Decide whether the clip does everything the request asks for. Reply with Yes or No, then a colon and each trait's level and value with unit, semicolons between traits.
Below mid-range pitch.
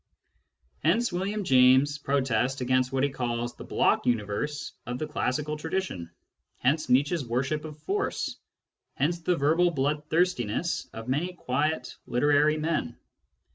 No: medium, 145 Hz